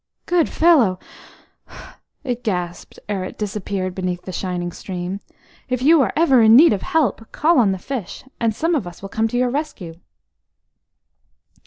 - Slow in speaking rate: No, average, 165 wpm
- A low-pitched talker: No, high, 220 Hz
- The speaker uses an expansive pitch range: Yes, wide, 6.6 semitones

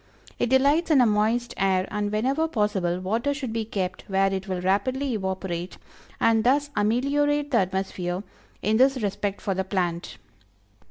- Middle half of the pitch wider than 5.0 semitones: Yes, wide, 5.4 semitones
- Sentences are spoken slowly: No, average, 160 wpm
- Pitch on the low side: No, high, 210 Hz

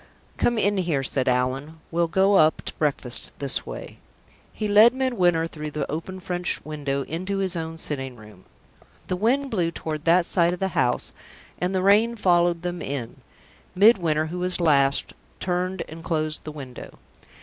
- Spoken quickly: No, average, 170 wpm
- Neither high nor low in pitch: Yes, medium, 170 Hz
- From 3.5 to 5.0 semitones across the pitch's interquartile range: Yes, average, 3.8 semitones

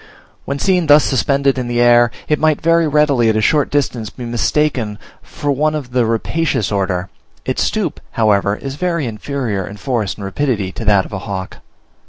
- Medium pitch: No, low, 125 Hz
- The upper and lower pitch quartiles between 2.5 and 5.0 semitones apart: No, wide, 5.5 semitones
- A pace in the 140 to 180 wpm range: No, average, 190 wpm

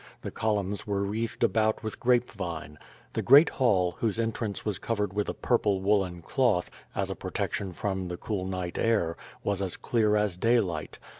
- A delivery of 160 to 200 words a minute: Yes, average, 175 wpm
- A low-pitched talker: Yes, low, 105 Hz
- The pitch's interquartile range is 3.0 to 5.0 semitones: Yes, average, 3.4 semitones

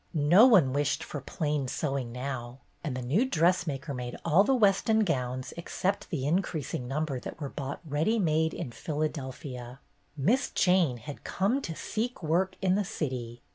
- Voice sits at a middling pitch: Yes, medium, 150 Hz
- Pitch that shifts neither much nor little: No, wide, 5.9 semitones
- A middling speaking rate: Yes, average, 165 wpm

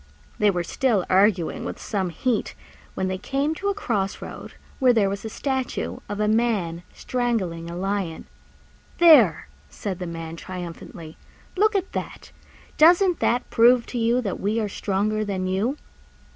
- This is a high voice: Yes, high, 210 Hz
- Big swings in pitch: No, average, 5.0 semitones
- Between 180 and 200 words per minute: No, average, 160 wpm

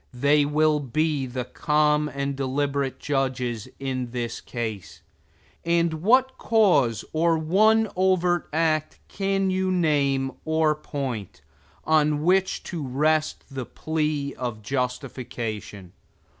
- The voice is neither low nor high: Yes, medium, 150 Hz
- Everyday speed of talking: No, slow, 115 wpm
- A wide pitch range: No, average, 3.8 semitones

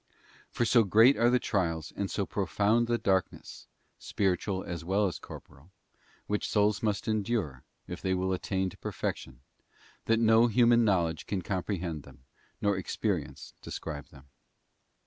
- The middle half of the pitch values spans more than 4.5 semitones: No, average, 4.0 semitones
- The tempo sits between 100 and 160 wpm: Yes, average, 150 wpm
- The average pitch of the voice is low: Yes, low, 100 Hz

